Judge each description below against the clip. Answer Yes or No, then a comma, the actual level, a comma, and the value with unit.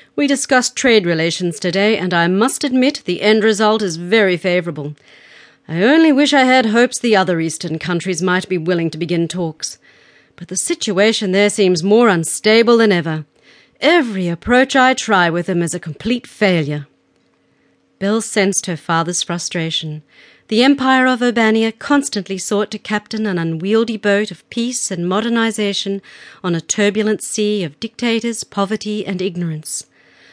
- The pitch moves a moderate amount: Yes, average, 4.4 semitones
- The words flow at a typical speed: Yes, average, 155 wpm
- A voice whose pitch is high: Yes, high, 205 Hz